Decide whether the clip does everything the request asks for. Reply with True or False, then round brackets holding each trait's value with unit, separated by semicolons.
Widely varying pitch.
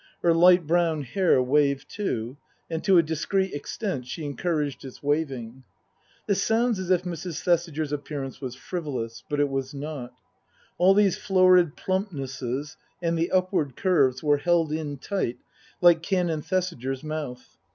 False (4.6 semitones)